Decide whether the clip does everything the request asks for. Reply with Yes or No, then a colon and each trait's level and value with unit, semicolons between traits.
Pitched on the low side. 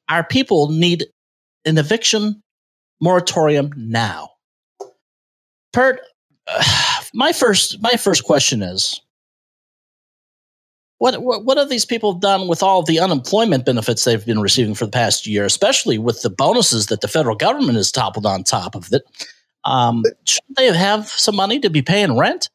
No: medium, 170 Hz